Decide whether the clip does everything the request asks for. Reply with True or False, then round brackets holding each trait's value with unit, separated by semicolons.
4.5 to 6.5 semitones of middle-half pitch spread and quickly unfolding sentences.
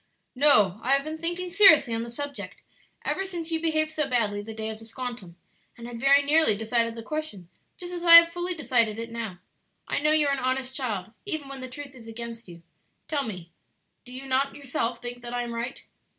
True (5.1 semitones; 220 wpm)